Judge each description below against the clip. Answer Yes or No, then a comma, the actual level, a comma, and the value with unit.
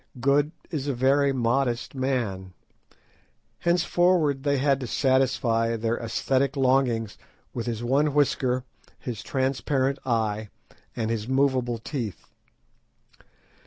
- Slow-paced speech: Yes, slow, 110 wpm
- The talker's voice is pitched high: No, low, 130 Hz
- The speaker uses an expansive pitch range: No, average, 3.1 semitones